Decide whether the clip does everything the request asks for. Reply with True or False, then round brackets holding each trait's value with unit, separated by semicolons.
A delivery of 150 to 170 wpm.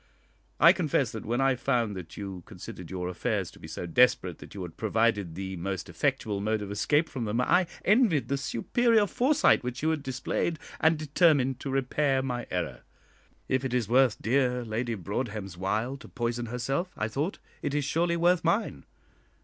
False (185 wpm)